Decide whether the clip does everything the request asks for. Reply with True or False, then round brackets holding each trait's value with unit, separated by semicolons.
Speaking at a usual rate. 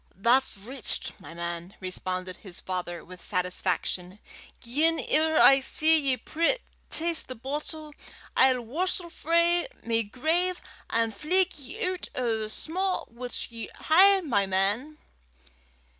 False (130 wpm)